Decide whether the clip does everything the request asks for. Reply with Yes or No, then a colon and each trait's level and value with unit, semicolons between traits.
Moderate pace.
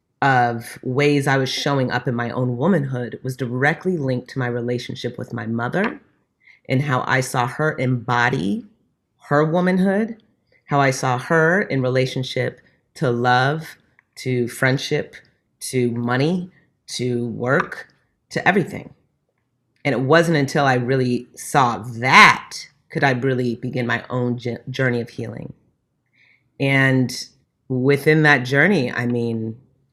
No: slow, 130 wpm